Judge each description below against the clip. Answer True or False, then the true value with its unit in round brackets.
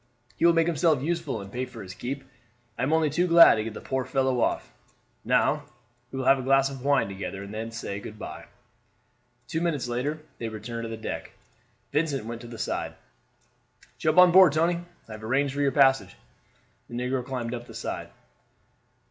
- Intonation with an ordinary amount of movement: True (4.8 semitones)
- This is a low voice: True (130 Hz)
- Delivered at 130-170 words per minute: False (200 wpm)